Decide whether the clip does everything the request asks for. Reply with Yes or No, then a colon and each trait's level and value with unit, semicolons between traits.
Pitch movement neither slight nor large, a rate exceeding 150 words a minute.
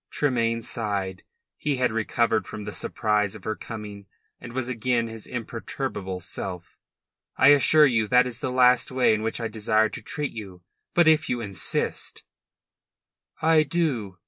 Yes: average, 3.3 semitones; average, 165 wpm